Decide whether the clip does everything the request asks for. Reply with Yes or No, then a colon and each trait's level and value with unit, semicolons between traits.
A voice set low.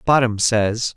Yes: low, 115 Hz